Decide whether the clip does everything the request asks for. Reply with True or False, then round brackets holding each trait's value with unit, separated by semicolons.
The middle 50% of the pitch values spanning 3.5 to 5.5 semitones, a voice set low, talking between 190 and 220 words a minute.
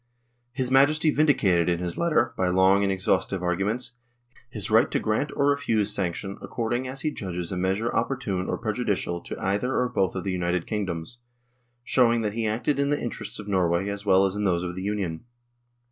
True (4.6 semitones; 100 Hz; 195 wpm)